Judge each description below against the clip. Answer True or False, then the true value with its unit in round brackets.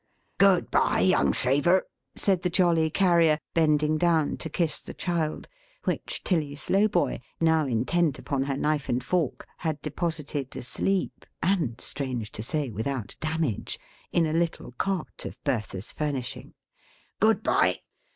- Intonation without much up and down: False (3.9 semitones)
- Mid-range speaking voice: True (155 Hz)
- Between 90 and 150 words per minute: True (140 wpm)